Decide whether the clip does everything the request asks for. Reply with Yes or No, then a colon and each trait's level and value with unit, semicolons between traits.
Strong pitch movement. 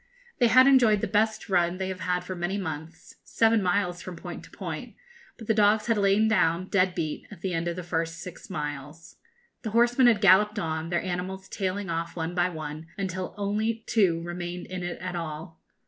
No: average, 3.5 semitones